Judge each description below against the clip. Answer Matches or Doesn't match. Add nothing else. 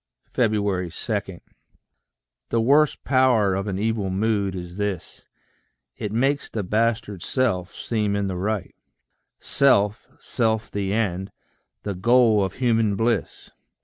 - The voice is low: Matches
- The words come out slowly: Matches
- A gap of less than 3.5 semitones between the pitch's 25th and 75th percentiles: Matches